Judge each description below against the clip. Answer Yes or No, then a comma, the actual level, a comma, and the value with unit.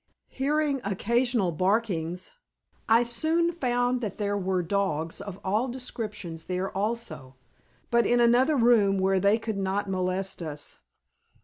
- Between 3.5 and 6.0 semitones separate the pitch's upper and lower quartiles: Yes, average, 4.5 semitones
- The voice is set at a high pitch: Yes, high, 205 Hz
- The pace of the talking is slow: Yes, slow, 130 wpm